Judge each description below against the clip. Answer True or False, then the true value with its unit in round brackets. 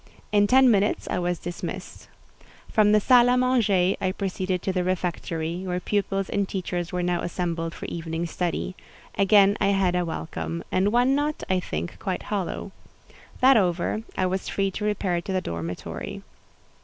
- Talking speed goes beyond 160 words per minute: True (170 wpm)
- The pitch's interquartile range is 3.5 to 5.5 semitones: False (2.7 semitones)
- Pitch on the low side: False (185 Hz)